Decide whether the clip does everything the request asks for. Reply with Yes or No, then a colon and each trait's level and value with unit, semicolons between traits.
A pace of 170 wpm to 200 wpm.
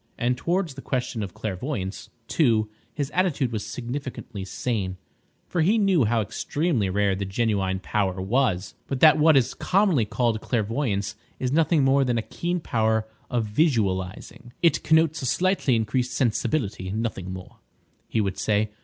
No: average, 155 wpm